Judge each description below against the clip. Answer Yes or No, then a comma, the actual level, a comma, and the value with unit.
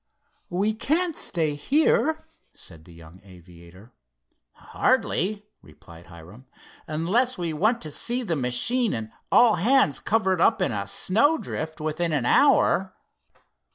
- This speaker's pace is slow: Yes, slow, 125 wpm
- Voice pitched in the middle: Yes, medium, 165 Hz